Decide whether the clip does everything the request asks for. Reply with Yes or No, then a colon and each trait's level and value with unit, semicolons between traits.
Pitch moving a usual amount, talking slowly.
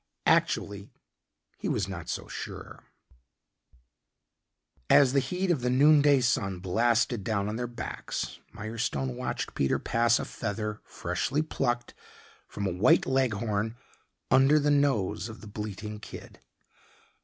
Yes: average, 4.1 semitones; slow, 130 wpm